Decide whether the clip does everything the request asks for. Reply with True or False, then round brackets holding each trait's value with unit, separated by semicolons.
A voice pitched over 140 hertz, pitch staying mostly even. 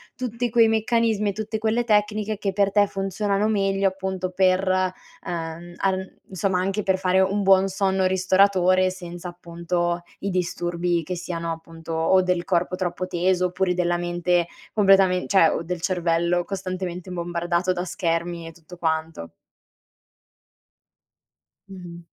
True (185 Hz; 2.0 semitones)